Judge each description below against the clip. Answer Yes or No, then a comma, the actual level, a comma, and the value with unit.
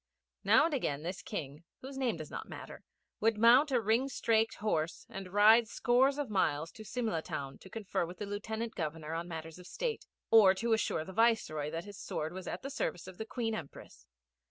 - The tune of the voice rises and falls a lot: Yes, wide, 5.9 semitones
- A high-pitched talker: Yes, high, 205 Hz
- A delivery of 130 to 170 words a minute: No, fast, 205 wpm